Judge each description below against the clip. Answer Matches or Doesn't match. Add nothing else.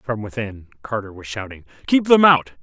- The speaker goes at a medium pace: Matches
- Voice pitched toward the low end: Matches